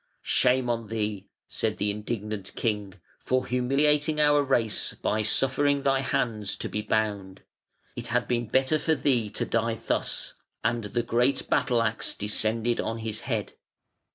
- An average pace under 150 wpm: No, average, 155 wpm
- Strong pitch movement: No, average, 3.6 semitones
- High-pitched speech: No, low, 115 Hz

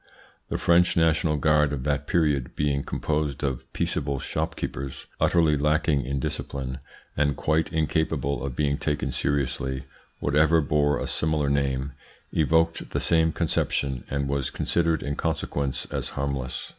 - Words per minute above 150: No, average, 140 wpm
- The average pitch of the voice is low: Yes, very low, 70 Hz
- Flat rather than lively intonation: Yes, narrow, 2.2 semitones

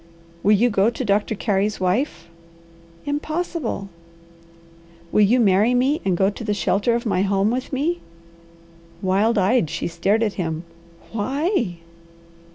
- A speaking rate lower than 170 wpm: Yes, average, 140 wpm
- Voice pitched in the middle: No, high, 210 Hz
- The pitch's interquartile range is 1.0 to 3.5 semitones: No, average, 4.3 semitones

